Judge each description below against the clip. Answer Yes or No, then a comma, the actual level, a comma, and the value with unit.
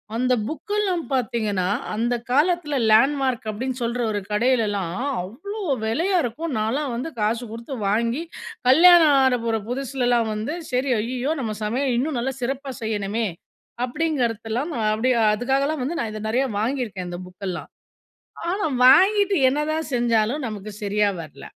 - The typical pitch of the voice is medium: No, high, 245 Hz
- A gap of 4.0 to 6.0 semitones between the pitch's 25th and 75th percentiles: Yes, average, 4.7 semitones